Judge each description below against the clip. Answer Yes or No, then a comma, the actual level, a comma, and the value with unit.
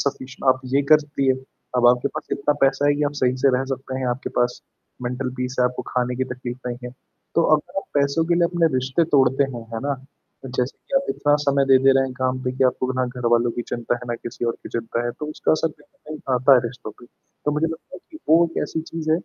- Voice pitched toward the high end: No, low, 130 Hz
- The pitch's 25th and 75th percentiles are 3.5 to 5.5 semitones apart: No, average, 2.9 semitones